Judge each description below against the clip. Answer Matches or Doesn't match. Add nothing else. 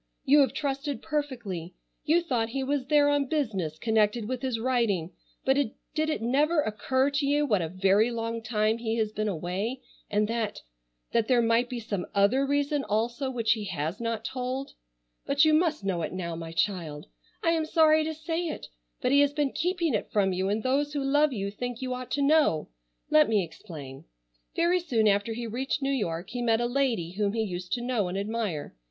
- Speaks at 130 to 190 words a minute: Doesn't match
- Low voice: Doesn't match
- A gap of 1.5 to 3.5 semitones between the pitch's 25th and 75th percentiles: Doesn't match